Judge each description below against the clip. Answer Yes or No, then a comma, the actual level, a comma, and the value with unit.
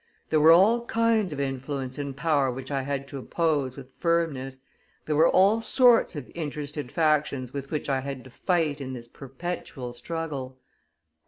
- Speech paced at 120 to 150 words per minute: No, average, 170 wpm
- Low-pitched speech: No, medium, 145 Hz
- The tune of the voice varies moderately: Yes, average, 3.8 semitones